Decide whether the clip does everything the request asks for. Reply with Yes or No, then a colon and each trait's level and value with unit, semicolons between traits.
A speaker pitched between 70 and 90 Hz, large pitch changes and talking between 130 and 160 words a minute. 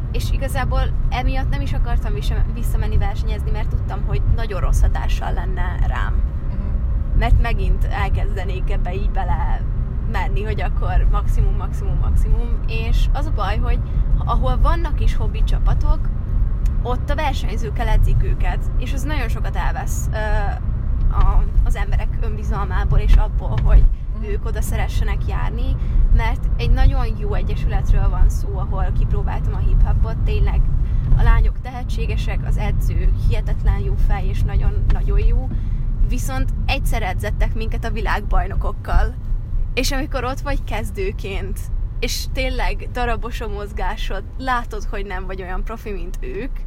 No: low, 105 Hz; wide, 6.7 semitones; average, 140 wpm